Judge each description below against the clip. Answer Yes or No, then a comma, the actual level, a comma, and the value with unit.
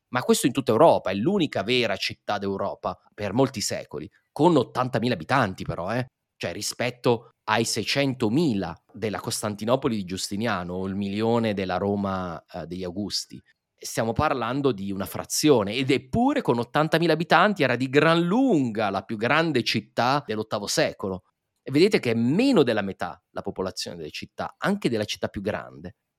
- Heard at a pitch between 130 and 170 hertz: No, low, 115 Hz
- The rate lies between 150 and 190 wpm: Yes, average, 160 wpm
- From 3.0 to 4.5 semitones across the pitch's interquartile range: No, average, 5.3 semitones